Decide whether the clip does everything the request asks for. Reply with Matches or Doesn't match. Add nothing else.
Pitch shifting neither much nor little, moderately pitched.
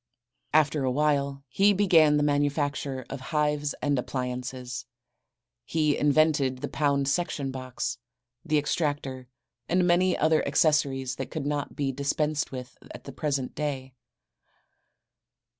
Doesn't match